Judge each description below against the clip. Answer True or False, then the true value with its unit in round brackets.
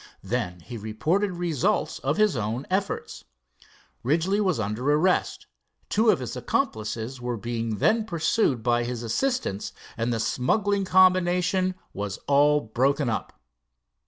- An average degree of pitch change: False (8.2 semitones)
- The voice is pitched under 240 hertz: True (140 Hz)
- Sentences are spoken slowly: True (130 wpm)